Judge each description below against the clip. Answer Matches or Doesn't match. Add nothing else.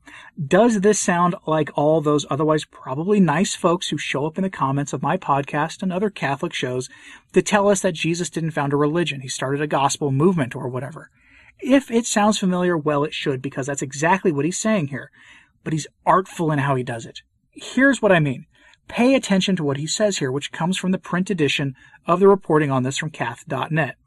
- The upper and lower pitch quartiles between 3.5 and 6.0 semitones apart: Matches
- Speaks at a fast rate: Matches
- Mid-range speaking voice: Matches